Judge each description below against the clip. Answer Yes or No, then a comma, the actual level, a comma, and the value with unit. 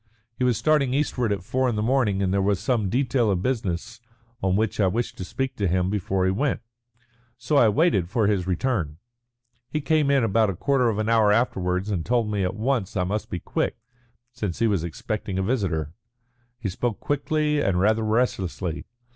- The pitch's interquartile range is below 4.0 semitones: No, average, 4.9 semitones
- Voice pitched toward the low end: Yes, low, 110 Hz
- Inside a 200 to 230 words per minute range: Yes, fast, 205 wpm